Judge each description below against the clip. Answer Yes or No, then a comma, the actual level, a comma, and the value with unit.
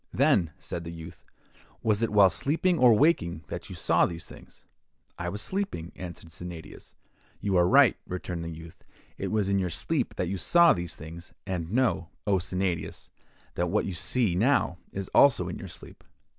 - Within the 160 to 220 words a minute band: Yes, average, 180 wpm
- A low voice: Yes, very low, 90 Hz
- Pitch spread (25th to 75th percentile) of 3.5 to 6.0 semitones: Yes, average, 3.9 semitones